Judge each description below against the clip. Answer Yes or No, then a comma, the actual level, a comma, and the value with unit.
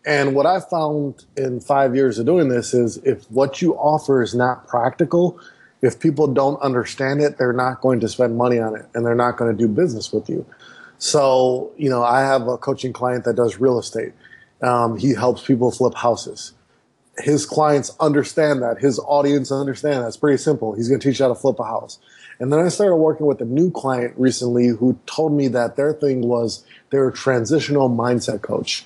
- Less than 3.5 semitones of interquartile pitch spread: Yes, average, 2.9 semitones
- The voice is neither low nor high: No, low, 130 Hz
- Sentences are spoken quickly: Yes, fast, 210 wpm